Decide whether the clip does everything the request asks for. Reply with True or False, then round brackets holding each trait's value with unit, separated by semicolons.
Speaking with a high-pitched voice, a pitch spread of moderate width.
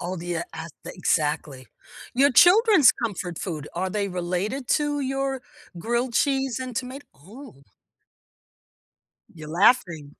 False (210 Hz; 7.8 semitones)